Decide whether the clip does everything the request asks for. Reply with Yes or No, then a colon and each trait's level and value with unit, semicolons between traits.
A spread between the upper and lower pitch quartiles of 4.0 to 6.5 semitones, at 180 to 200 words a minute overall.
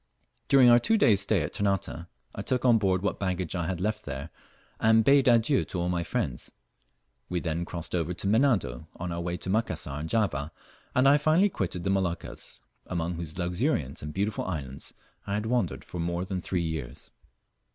Yes: average, 4.7 semitones; average, 195 wpm